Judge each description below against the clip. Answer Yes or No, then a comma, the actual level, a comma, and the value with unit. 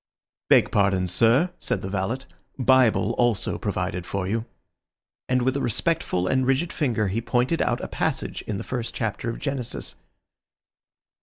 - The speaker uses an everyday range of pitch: Yes, average, 4.5 semitones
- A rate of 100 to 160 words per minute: Yes, average, 155 wpm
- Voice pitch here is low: Yes, low, 120 Hz